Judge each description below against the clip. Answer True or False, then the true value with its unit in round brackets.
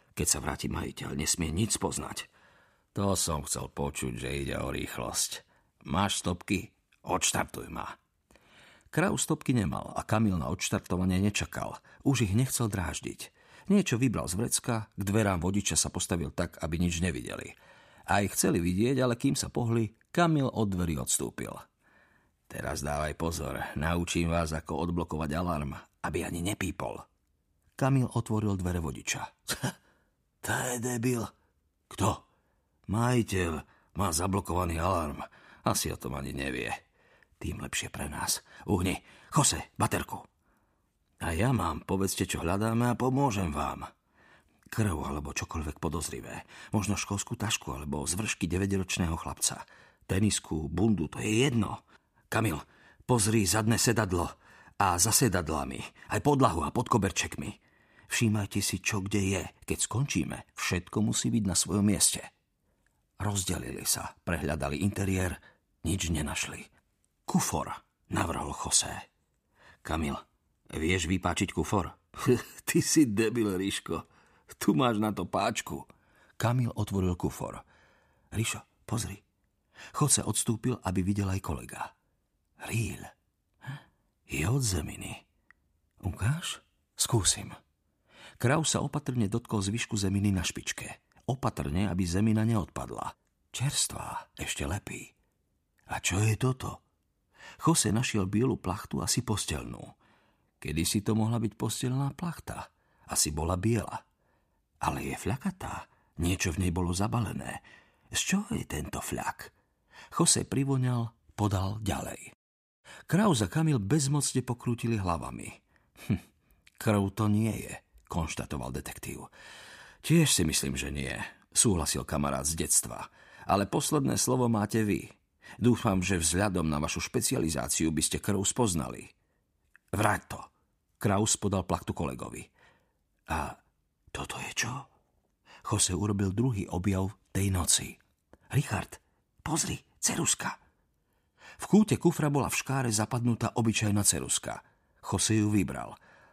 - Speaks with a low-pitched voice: True (100 Hz)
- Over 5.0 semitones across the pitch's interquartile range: True (5.5 semitones)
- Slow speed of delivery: False (125 wpm)